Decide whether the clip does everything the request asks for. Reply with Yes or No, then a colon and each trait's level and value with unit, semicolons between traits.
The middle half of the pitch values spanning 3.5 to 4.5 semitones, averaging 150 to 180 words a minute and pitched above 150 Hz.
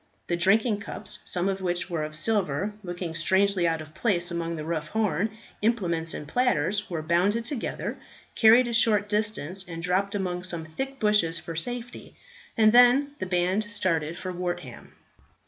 Yes: average, 4.1 semitones; average, 165 wpm; medium, 185 Hz